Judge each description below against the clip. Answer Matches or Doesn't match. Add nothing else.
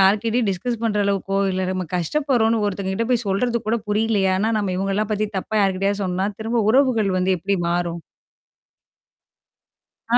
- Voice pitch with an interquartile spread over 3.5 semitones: Doesn't match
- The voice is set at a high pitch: Matches